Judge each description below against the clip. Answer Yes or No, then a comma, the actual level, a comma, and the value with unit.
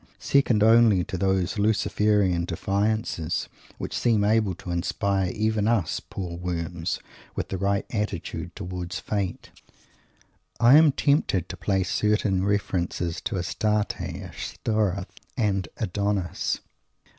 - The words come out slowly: Yes, slow, 115 wpm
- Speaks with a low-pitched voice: Yes, low, 100 Hz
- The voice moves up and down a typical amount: Yes, average, 3.0 semitones